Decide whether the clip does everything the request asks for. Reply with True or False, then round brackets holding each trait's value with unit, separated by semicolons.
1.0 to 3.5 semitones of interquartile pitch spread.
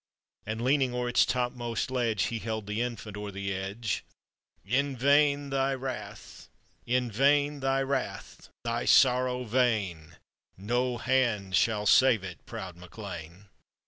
False (4.0 semitones)